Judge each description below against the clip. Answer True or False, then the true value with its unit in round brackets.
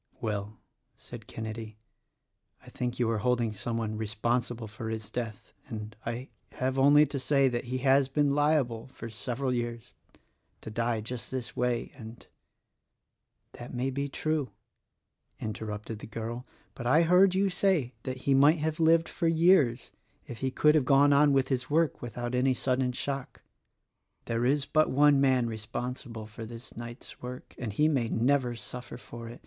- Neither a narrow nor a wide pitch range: True (3.4 semitones)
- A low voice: True (125 Hz)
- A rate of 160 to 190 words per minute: True (180 wpm)